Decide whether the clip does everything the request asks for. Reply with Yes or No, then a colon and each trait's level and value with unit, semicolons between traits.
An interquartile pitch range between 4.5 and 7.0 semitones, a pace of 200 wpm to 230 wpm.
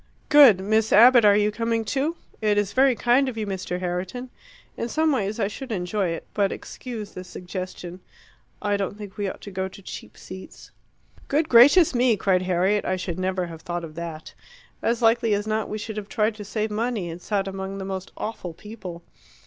No: average, 3.6 semitones; fast, 205 wpm